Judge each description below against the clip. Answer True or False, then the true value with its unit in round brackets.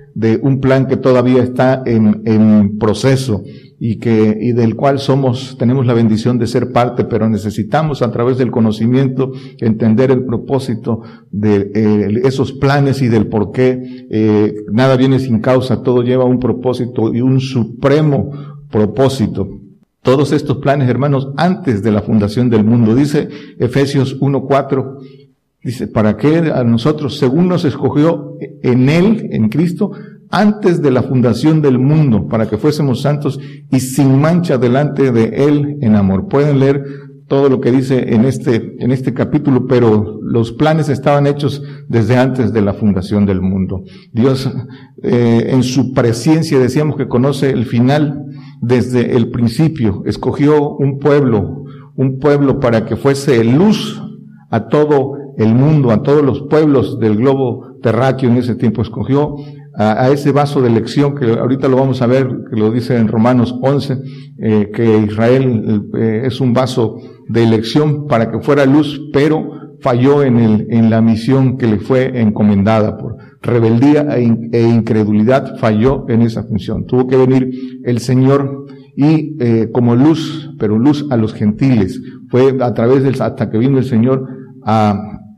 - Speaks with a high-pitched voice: False (130 Hz)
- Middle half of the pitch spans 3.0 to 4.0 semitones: True (3.5 semitones)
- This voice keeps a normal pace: True (160 wpm)